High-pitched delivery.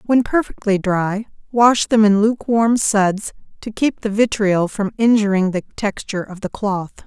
Yes: high, 210 Hz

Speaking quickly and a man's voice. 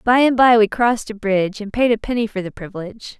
No: fast, 265 wpm; female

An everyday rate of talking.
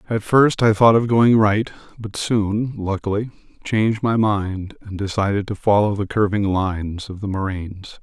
Yes: average, 170 wpm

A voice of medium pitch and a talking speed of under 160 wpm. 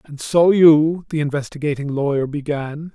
Yes: medium, 150 Hz; average, 140 wpm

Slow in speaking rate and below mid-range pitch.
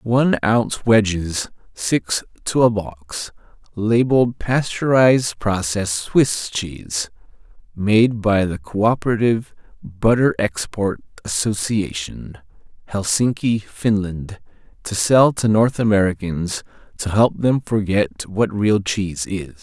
Yes: slow, 105 wpm; low, 105 Hz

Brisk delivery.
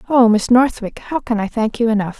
Yes: fast, 245 wpm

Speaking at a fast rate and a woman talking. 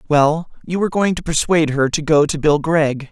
No: fast, 230 wpm; male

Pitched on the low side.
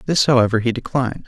Yes: low, 125 Hz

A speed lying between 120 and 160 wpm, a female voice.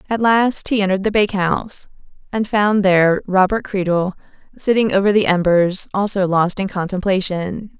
Yes: average, 145 wpm; female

